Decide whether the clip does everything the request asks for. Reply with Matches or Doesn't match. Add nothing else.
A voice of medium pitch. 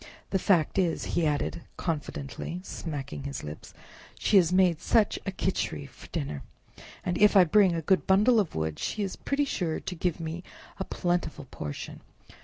Matches